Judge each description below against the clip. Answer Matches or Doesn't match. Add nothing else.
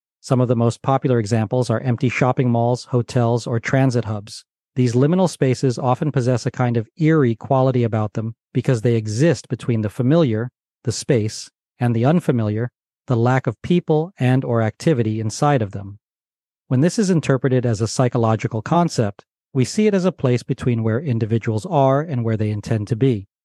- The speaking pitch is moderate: Doesn't match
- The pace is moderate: Matches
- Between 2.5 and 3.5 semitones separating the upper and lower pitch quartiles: Matches